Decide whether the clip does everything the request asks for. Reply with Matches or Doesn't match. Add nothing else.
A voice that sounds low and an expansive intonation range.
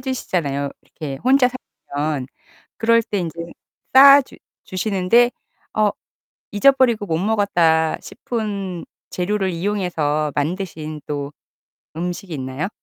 Doesn't match